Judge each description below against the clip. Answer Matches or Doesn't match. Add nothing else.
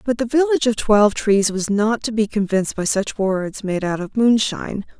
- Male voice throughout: Doesn't match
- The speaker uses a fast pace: Matches